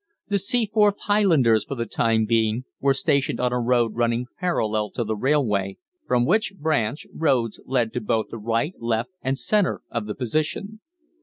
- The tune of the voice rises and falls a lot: Yes, wide, 5.8 semitones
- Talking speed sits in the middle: Yes, average, 170 wpm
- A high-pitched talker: No, low, 125 Hz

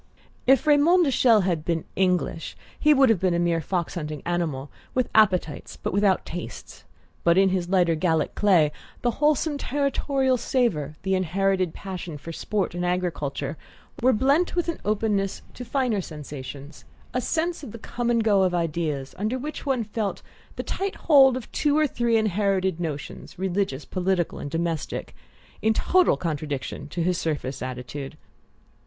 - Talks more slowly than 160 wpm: No, average, 165 wpm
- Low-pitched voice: No, high, 190 Hz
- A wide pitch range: Yes, wide, 6.8 semitones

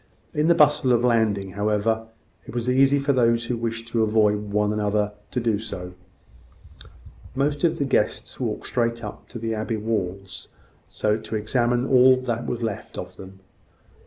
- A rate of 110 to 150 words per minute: No, average, 165 wpm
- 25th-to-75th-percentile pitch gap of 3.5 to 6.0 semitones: No, average, 2.9 semitones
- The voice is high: No, low, 115 Hz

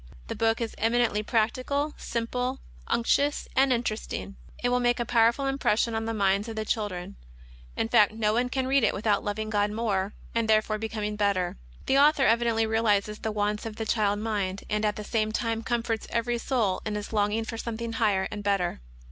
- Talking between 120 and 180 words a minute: No, average, 195 wpm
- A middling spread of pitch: No, narrow, 2.1 semitones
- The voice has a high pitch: Yes, high, 220 Hz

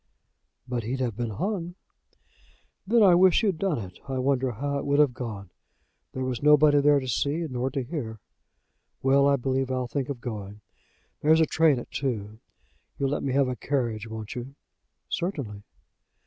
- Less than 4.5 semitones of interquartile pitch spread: Yes, average, 3.4 semitones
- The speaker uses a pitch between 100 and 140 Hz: Yes, low, 135 Hz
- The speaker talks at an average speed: Yes, average, 175 wpm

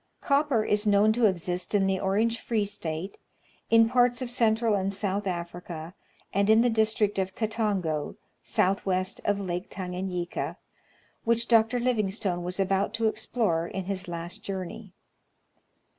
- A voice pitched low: No, high, 200 Hz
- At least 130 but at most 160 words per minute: Yes, average, 145 wpm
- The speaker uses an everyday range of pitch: Yes, average, 3.4 semitones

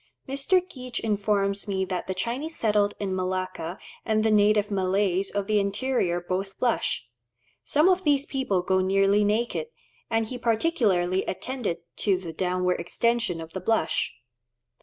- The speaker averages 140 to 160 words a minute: Yes, average, 150 wpm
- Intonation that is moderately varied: Yes, average, 4.0 semitones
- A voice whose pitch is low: No, high, 200 Hz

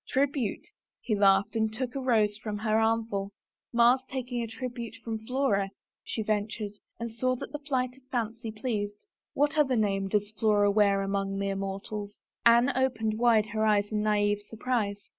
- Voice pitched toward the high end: Yes, high, 220 Hz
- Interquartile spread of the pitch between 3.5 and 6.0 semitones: No, average, 2.9 semitones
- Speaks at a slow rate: No, average, 175 wpm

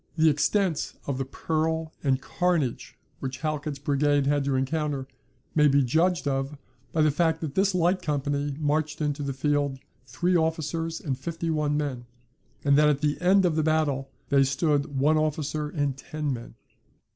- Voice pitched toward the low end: No, medium, 150 Hz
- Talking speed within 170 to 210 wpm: Yes, average, 175 wpm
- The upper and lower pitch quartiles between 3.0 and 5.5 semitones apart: No, narrow, 2.4 semitones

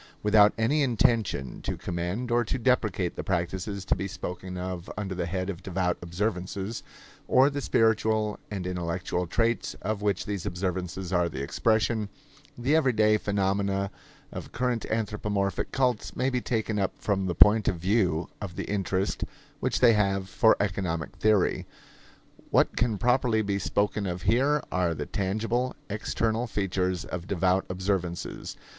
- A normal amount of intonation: Yes, average, 3.4 semitones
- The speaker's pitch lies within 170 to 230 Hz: No, low, 100 Hz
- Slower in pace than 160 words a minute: Yes, average, 150 wpm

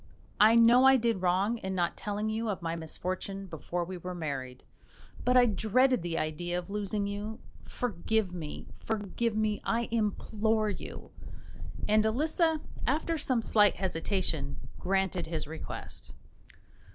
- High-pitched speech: Yes, high, 205 Hz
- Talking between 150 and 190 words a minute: No, average, 140 wpm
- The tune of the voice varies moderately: Yes, average, 4.1 semitones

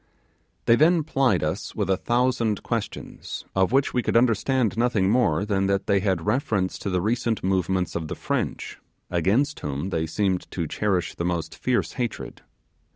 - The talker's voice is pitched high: No, low, 100 Hz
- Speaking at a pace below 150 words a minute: No, average, 170 wpm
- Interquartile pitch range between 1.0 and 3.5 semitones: No, average, 4.8 semitones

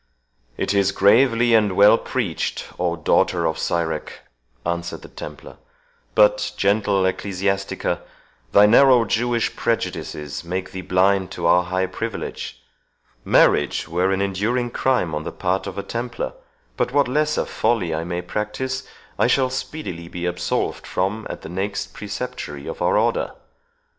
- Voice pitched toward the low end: Yes, low, 100 Hz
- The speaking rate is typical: Yes, average, 145 wpm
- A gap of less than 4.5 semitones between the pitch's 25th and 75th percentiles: No, average, 4.9 semitones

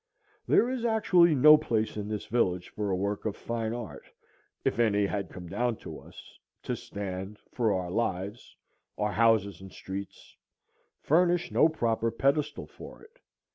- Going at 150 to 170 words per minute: Yes, average, 160 wpm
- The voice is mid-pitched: No, low, 110 Hz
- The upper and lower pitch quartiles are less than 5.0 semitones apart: No, wide, 5.6 semitones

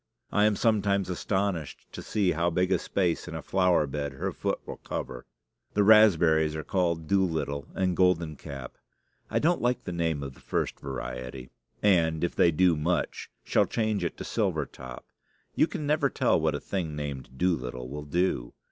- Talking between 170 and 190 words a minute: Yes, average, 185 wpm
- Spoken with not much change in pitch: No, average, 4.7 semitones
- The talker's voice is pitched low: Yes, very low, 85 Hz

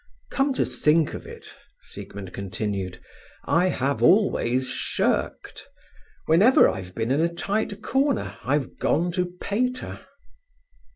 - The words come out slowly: Yes, slow, 120 wpm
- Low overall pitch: No, medium, 165 Hz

